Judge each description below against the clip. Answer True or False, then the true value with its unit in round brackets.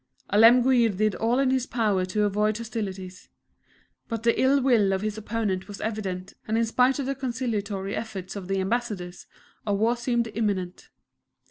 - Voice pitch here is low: False (215 Hz)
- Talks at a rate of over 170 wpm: False (165 wpm)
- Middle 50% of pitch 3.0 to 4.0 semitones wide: True (3.5 semitones)